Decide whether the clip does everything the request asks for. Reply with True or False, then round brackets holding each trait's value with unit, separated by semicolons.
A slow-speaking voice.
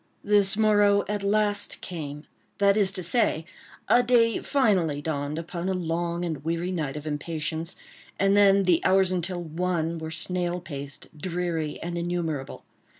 False (150 wpm)